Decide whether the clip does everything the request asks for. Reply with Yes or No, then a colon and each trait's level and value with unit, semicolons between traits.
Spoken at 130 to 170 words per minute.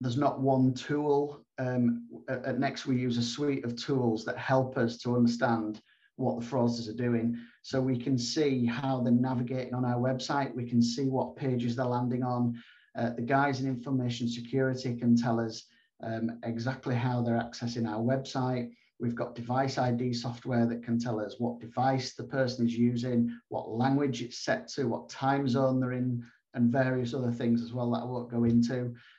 No: average, 190 wpm